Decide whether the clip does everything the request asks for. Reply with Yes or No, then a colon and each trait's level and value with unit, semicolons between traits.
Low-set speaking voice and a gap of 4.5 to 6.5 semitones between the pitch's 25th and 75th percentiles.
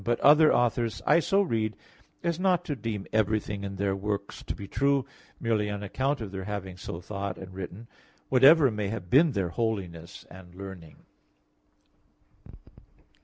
Yes: low, 105 Hz; average, 5.1 semitones